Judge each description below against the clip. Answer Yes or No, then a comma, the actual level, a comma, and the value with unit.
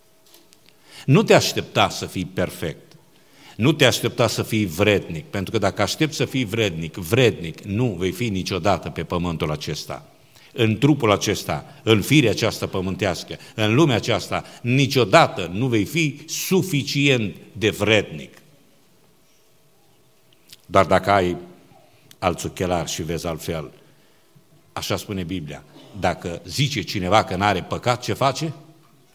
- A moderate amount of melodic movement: No, wide, 5.9 semitones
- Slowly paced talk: No, average, 130 wpm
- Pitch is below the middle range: Yes, low, 110 Hz